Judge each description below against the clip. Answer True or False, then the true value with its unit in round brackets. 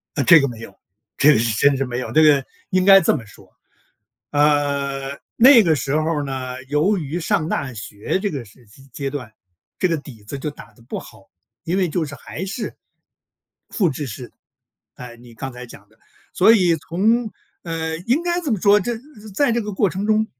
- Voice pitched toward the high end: False (150 Hz)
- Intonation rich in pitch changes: True (6.5 semitones)